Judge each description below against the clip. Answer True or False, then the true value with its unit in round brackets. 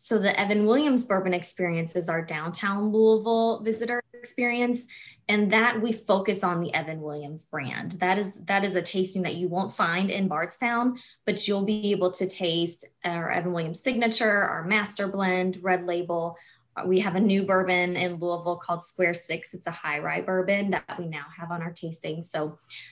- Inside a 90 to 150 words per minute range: False (185 wpm)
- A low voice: False (185 Hz)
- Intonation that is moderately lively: True (3.4 semitones)